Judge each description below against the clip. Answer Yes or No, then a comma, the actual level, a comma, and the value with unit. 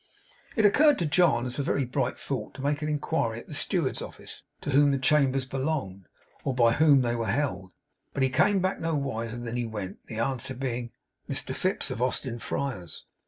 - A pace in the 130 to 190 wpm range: No, average, 200 wpm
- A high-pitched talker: No, low, 130 Hz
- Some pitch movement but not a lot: Yes, average, 3.8 semitones